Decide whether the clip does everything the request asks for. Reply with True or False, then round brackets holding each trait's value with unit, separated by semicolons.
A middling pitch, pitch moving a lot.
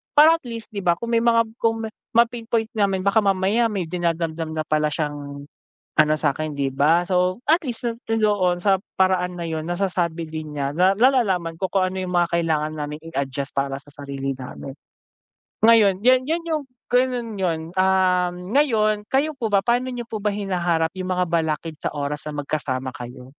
True (180 Hz; 6.1 semitones)